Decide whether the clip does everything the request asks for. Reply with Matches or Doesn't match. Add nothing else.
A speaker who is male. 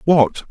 Matches